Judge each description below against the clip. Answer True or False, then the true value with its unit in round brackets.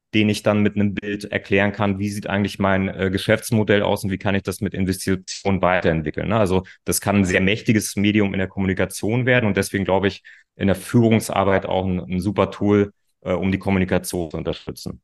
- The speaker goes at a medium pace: False (210 wpm)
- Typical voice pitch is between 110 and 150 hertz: False (100 Hz)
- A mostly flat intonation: True (1.4 semitones)